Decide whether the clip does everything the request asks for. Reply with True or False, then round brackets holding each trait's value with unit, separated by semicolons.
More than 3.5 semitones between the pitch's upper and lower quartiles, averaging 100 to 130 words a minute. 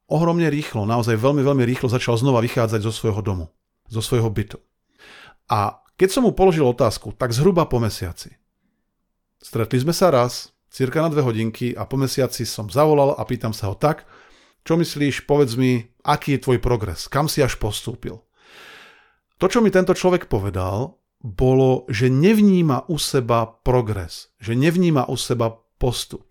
False (4.8 semitones; 165 wpm)